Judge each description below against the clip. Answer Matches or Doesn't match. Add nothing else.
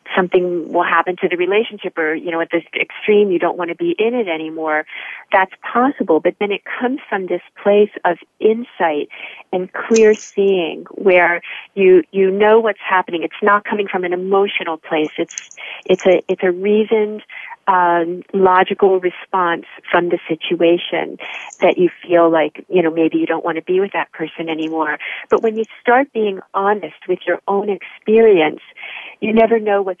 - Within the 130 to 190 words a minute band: Matches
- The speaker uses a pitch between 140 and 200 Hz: Matches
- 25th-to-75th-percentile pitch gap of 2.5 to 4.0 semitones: Matches